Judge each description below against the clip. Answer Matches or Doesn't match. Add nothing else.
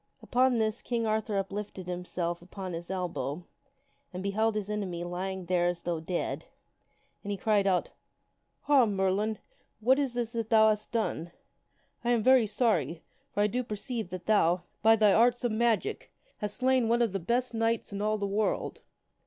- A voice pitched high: Matches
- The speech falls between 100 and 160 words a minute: Doesn't match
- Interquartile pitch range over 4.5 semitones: Doesn't match